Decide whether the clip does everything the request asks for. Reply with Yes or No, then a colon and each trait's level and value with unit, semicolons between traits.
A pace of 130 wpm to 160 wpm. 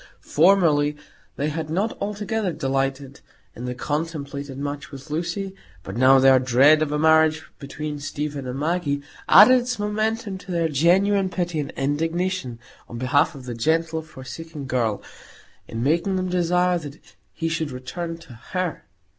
Yes: average, 155 wpm